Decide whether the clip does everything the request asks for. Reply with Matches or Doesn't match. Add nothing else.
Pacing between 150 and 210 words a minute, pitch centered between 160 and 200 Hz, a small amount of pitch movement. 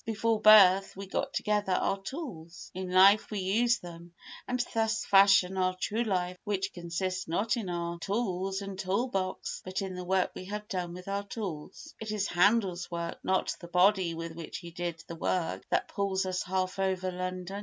Matches